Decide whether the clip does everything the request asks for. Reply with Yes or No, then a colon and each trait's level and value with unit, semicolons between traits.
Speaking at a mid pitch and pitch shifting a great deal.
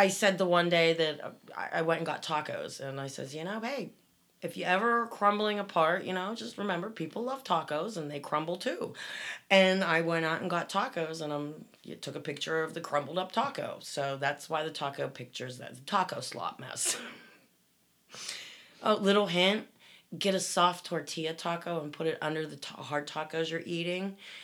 No: medium, 170 Hz; average, 3.7 semitones